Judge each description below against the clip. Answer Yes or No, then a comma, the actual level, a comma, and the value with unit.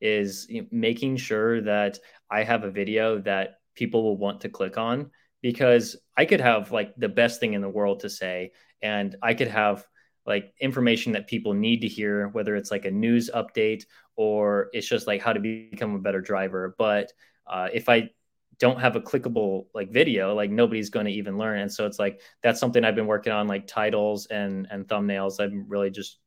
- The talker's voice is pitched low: Yes, low, 105 Hz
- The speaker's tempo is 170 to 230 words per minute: Yes, fast, 205 wpm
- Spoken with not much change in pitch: Yes, narrow, 2.0 semitones